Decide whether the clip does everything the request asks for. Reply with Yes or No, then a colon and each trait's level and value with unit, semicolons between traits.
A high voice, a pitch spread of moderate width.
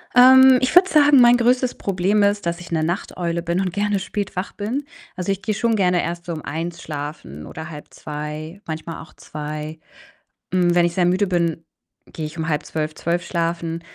No: medium, 175 Hz; average, 4.1 semitones